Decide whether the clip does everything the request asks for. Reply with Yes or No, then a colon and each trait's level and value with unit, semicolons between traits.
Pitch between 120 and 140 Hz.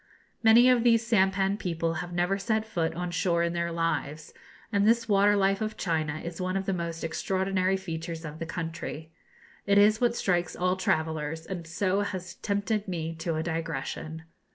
No: medium, 180 Hz